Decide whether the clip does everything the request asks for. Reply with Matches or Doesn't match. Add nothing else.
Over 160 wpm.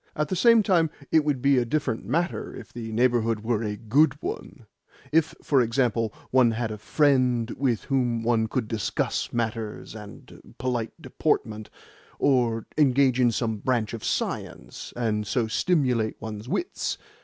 Doesn't match